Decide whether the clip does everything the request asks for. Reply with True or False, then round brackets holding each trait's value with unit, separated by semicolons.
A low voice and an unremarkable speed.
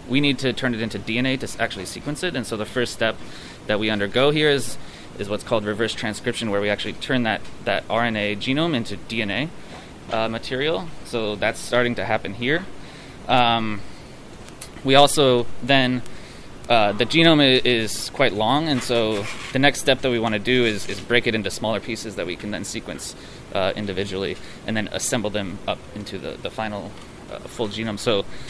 True (115 Hz; 195 wpm)